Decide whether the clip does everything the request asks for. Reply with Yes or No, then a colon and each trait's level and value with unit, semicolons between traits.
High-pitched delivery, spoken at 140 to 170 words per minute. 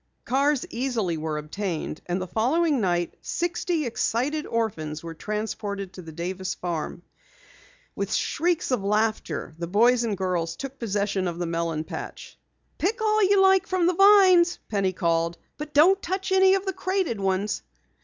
Yes: high, 220 Hz; average, 160 wpm